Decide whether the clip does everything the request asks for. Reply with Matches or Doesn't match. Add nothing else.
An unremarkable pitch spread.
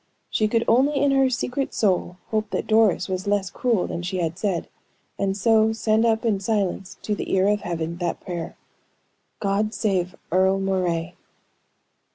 Matches